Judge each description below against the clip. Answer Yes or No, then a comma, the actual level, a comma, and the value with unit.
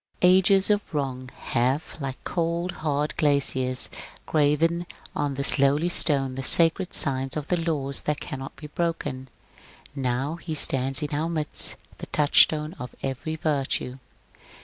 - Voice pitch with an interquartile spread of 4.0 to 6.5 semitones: No, average, 3.5 semitones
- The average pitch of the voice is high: No, medium, 145 Hz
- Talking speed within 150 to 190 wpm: No, average, 140 wpm